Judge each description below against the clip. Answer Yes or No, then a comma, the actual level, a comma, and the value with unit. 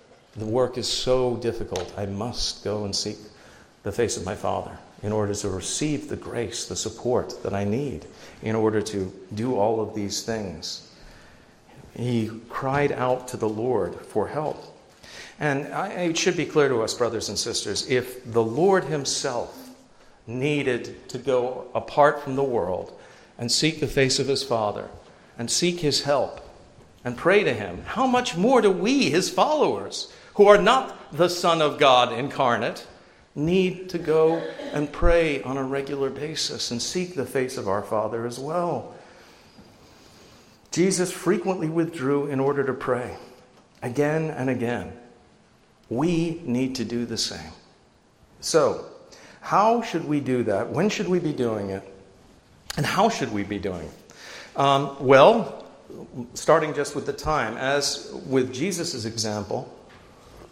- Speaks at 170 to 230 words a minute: No, average, 155 wpm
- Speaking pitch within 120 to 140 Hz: Yes, low, 135 Hz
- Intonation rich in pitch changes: Yes, wide, 6.3 semitones